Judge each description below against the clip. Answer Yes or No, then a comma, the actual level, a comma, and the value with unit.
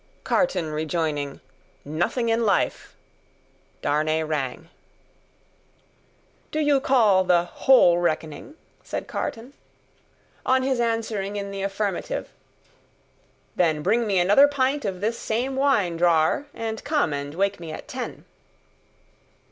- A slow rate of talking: Yes, slow, 115 wpm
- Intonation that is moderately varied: No, wide, 6.7 semitones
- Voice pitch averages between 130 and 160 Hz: No, high, 200 Hz